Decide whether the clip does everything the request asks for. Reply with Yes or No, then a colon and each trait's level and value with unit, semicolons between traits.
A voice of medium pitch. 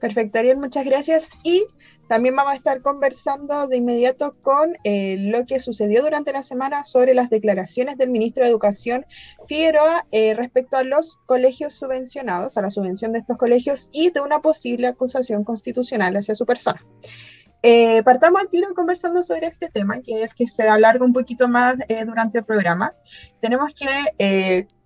No: very high, 250 Hz